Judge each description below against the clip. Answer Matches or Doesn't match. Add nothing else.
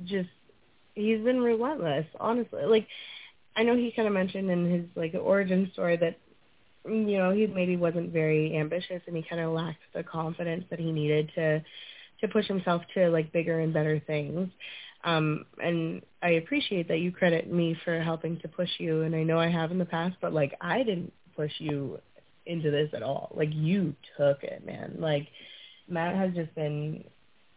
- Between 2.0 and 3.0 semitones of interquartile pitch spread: Matches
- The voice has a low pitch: Doesn't match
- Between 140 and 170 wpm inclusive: Doesn't match